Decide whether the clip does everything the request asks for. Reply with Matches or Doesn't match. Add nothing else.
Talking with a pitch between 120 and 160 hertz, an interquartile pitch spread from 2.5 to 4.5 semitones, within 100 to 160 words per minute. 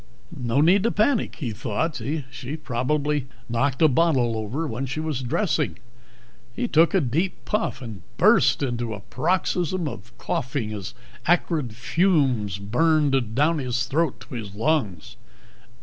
Doesn't match